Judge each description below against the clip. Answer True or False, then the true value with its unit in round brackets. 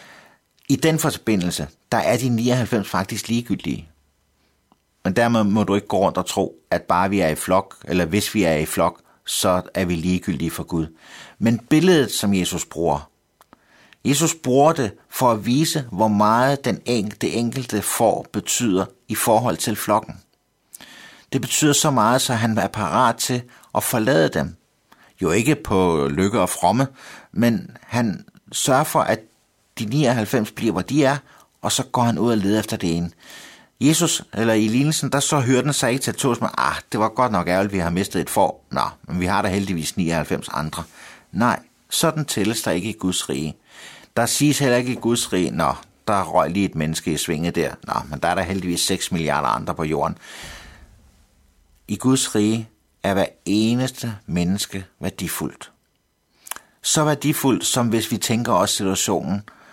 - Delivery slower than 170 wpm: False (185 wpm)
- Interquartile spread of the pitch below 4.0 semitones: False (5.6 semitones)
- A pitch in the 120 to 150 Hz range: False (110 Hz)